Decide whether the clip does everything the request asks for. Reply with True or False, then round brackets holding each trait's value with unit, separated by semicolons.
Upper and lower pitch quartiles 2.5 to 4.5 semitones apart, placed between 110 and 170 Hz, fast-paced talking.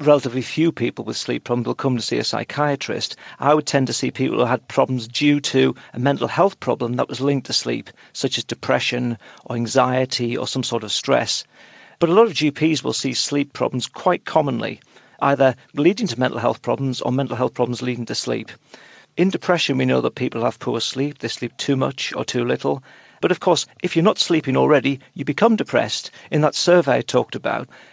True (3.4 semitones; 135 Hz; 215 wpm)